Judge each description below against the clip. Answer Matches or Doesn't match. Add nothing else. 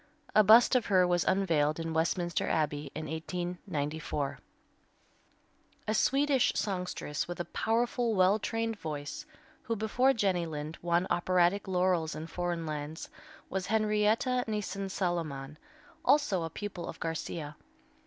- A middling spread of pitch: Matches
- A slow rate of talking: Matches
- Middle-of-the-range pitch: Matches